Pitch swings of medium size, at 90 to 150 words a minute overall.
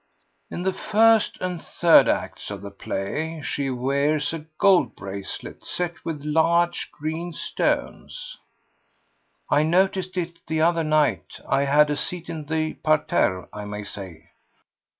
Yes: average, 3.9 semitones; average, 140 wpm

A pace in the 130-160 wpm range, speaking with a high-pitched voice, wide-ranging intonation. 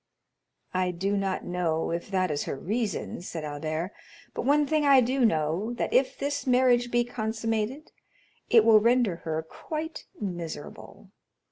Yes: average, 150 wpm; high, 215 Hz; wide, 6.4 semitones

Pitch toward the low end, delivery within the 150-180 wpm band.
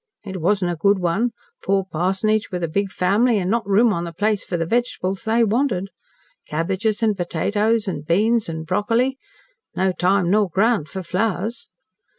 No: high, 195 Hz; average, 170 wpm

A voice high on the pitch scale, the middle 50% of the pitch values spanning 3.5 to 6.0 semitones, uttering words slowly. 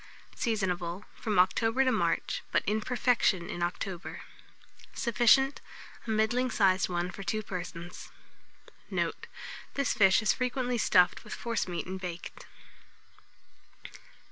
Yes: high, 210 Hz; average, 4.9 semitones; slow, 115 wpm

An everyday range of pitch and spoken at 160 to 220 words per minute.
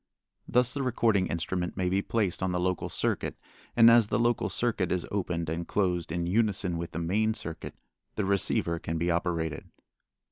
Yes: average, 4.2 semitones; average, 180 wpm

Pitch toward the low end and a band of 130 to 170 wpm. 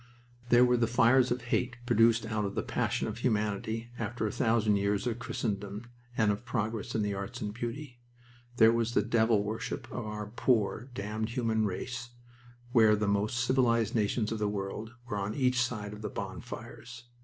No: low, 110 Hz; average, 185 wpm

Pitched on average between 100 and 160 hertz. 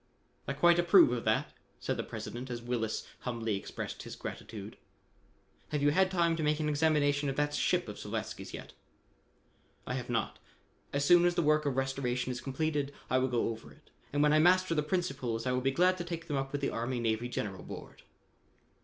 Yes: medium, 140 Hz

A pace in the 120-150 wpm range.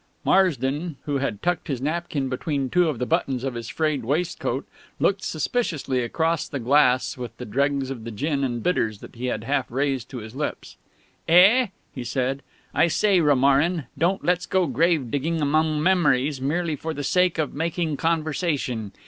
No: average, 175 wpm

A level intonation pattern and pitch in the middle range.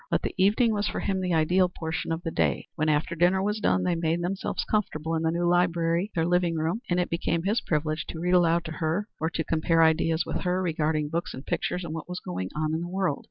Yes: narrow, 2.0 semitones; medium, 170 Hz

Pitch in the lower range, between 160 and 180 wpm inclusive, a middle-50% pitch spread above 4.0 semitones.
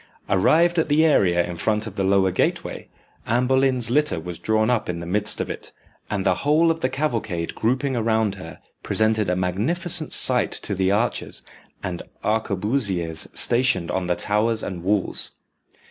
Yes: low, 110 Hz; average, 170 wpm; wide, 5.6 semitones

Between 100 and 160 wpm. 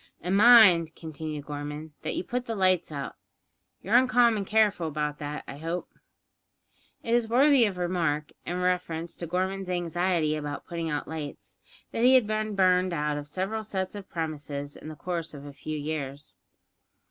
No: average, 170 wpm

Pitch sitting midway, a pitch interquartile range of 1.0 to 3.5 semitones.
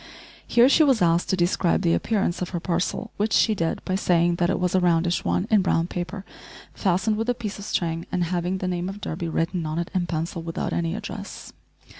Yes: medium, 180 Hz; average, 2.7 semitones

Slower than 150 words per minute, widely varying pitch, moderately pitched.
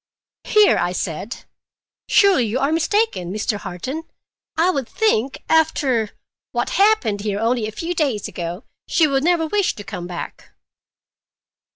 No: average, 140 wpm; wide, 8.1 semitones; very high, 260 Hz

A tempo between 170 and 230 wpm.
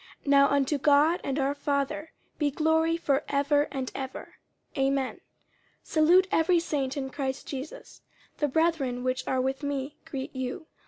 No: average, 160 wpm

